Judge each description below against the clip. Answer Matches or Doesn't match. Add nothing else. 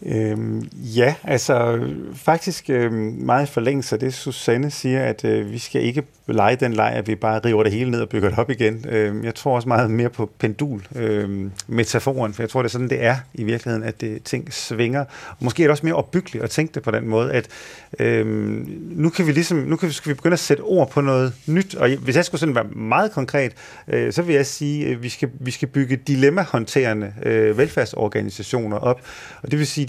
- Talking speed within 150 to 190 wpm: Doesn't match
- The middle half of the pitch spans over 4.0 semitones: Matches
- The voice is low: Matches